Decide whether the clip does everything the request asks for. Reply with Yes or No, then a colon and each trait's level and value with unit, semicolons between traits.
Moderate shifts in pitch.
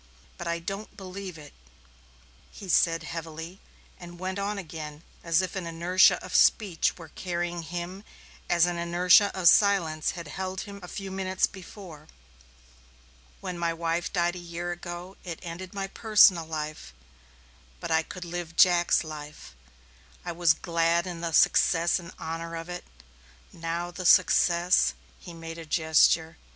No: narrow, 1.9 semitones